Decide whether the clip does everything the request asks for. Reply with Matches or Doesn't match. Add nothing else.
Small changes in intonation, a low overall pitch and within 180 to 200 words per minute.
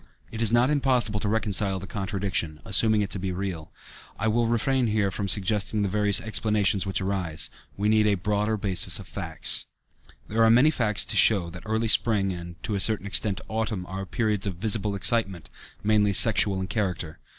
Matches